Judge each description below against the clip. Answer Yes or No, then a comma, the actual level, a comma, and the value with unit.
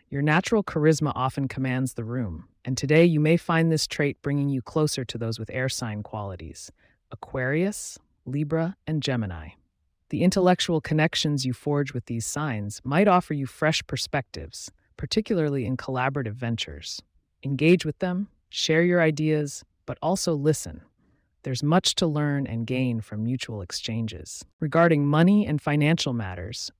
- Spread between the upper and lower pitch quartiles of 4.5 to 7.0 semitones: Yes, average, 5.1 semitones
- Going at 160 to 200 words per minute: No, average, 150 wpm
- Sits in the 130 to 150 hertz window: Yes, medium, 140 Hz